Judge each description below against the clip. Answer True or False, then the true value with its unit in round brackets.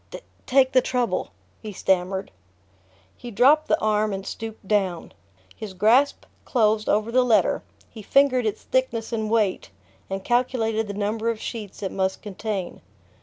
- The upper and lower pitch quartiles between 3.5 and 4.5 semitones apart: False (3.1 semitones)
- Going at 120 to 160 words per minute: True (150 wpm)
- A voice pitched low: False (220 Hz)